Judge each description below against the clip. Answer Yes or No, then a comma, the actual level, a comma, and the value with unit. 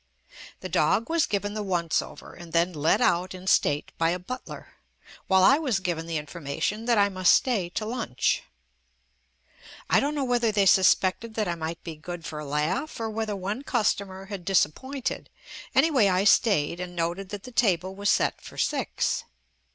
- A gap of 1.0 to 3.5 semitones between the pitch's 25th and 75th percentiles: No, average, 4.4 semitones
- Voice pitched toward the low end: No, high, 190 Hz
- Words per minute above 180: Yes, average, 190 wpm